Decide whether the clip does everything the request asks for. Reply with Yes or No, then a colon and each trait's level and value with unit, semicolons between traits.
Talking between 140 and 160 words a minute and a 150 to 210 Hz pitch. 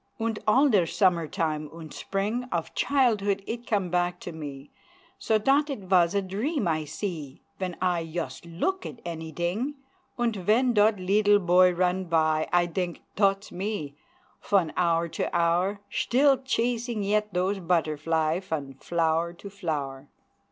Yes: average, 150 wpm; medium, 185 Hz